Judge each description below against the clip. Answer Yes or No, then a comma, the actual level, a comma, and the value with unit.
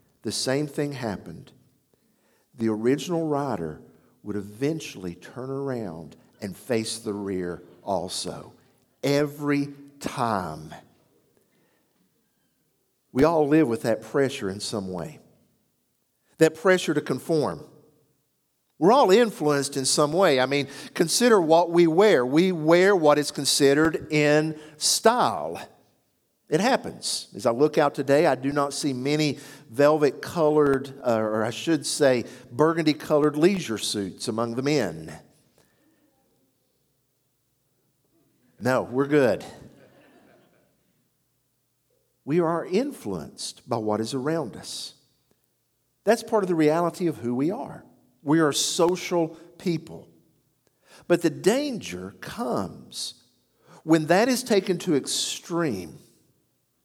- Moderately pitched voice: Yes, medium, 145 Hz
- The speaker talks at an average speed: No, slow, 115 wpm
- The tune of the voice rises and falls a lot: No, average, 4.4 semitones